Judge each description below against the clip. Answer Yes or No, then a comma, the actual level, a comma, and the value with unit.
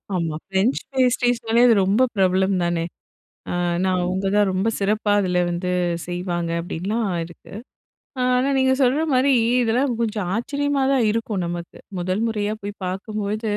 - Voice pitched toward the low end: No, high, 205 Hz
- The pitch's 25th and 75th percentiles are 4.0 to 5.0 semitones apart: Yes, average, 4.5 semitones